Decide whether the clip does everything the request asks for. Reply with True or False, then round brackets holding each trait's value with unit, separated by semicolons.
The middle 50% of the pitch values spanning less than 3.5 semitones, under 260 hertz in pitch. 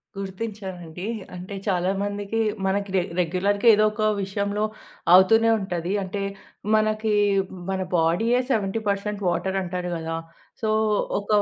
True (2.6 semitones; 200 Hz)